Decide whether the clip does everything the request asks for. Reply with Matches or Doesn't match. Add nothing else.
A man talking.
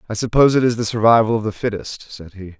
Matches